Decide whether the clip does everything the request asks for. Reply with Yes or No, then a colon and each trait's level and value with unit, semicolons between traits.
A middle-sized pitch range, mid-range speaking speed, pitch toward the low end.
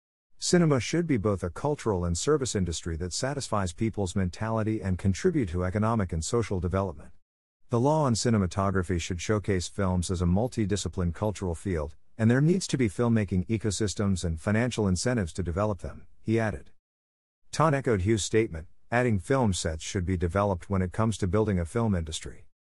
Yes: average, 4.1 semitones; average, 170 wpm; low, 100 Hz